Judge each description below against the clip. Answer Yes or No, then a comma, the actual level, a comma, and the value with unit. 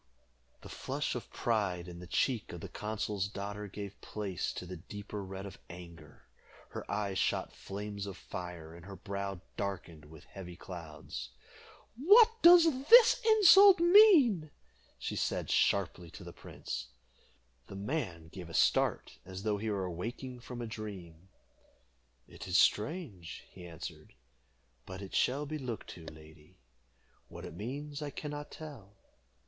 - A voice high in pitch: No, low, 100 Hz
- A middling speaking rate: Yes, average, 155 wpm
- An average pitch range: No, wide, 6.8 semitones